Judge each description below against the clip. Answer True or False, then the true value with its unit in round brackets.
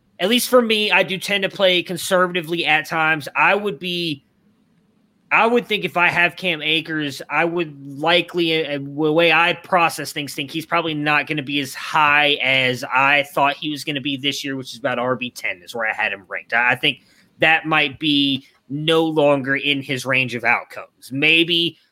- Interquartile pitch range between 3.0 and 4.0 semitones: True (3.7 semitones)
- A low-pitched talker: False (155 Hz)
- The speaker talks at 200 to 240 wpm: True (205 wpm)